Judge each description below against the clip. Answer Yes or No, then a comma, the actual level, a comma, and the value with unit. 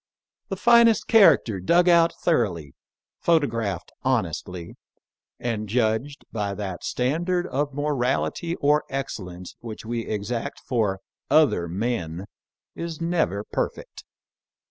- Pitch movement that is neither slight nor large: No, wide, 7.9 semitones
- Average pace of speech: No, slow, 110 wpm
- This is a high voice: No, low, 120 Hz